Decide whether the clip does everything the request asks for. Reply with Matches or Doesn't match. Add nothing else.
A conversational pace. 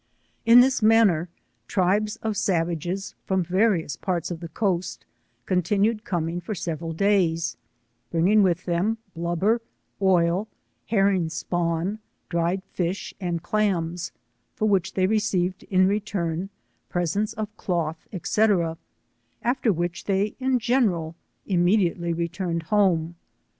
Doesn't match